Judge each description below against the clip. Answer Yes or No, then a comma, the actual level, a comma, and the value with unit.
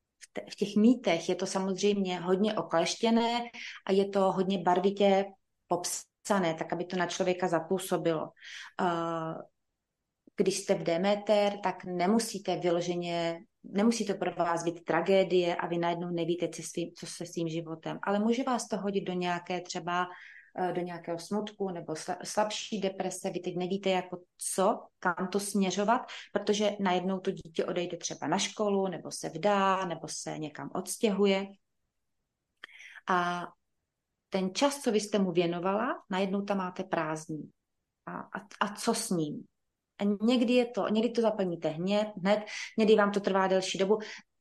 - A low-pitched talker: No, high, 190 Hz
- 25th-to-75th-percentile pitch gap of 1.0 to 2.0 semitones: No, average, 2.8 semitones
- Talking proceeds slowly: No, average, 155 wpm